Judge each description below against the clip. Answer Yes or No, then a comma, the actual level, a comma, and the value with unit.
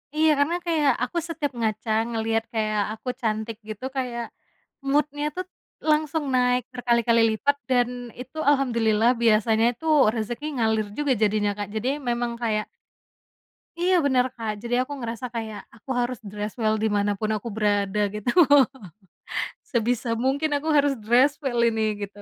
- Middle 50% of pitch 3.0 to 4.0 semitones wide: Yes, average, 3.6 semitones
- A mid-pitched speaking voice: No, high, 235 Hz